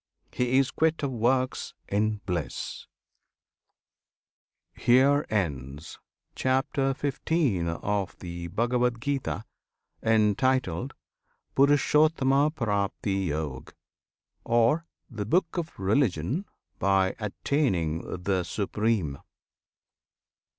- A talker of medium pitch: No, low, 115 Hz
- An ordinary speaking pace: No, slow, 75 wpm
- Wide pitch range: Yes, wide, 6.3 semitones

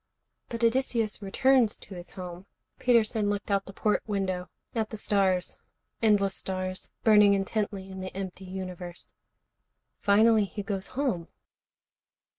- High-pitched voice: Yes, high, 200 Hz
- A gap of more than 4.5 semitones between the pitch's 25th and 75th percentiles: No, narrow, 2.5 semitones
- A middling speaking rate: No, slow, 130 wpm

